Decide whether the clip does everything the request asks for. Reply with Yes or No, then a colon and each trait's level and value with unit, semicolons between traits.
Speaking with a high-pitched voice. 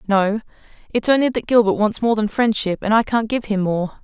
Yes: high, 215 Hz